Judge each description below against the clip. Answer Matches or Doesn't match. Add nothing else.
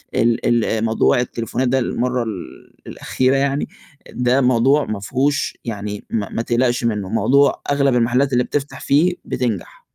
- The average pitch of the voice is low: Matches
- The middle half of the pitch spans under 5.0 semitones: Matches